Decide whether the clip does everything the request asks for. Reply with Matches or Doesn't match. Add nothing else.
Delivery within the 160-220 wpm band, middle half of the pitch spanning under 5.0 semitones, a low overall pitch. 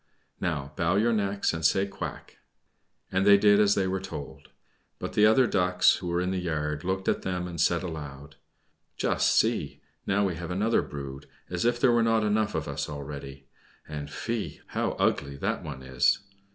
Doesn't match